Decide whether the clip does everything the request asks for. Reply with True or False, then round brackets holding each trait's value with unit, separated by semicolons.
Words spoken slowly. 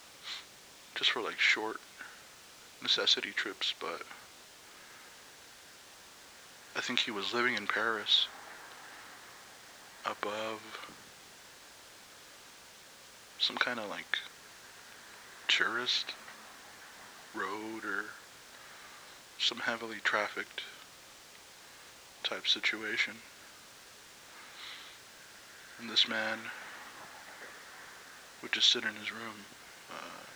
True (70 wpm)